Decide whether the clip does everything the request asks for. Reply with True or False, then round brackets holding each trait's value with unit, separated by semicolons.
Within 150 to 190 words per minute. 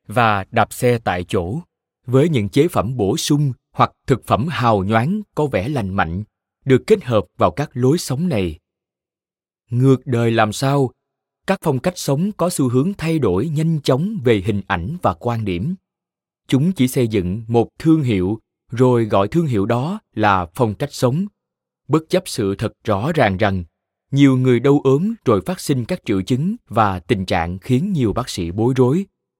True (185 wpm)